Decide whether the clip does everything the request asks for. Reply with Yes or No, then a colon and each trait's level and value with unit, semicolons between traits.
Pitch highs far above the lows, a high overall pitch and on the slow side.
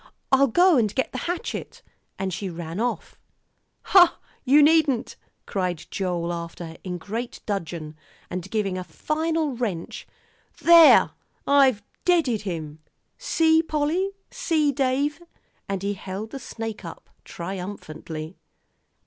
Yes: wide, 8.5 semitones; high, 220 Hz; slow, 130 wpm